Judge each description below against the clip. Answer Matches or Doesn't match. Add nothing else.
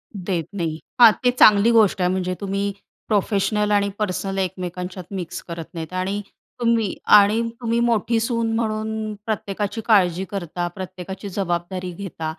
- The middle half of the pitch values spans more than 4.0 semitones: Doesn't match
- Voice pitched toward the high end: Matches